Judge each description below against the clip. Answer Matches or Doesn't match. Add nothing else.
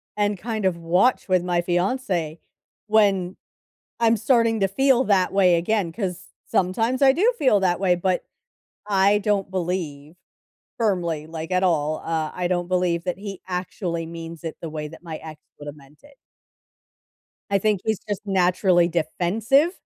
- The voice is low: Doesn't match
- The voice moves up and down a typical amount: Matches